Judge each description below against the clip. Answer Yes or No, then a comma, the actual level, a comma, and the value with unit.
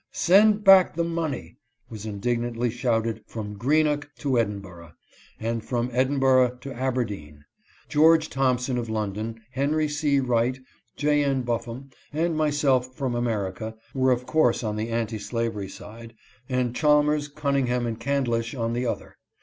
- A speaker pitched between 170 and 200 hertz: No, low, 125 Hz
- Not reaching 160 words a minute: Yes, average, 150 wpm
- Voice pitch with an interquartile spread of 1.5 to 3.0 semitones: No, average, 3.8 semitones